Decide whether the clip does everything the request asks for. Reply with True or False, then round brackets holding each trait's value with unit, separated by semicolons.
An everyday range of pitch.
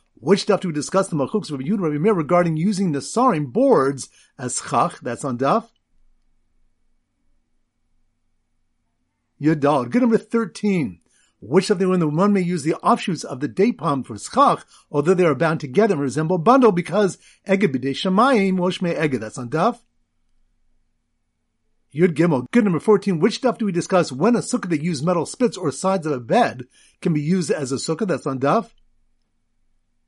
False (6.7 semitones)